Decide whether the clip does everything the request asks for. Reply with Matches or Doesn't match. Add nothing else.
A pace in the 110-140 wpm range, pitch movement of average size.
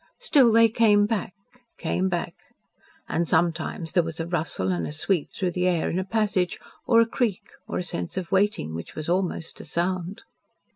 Doesn't match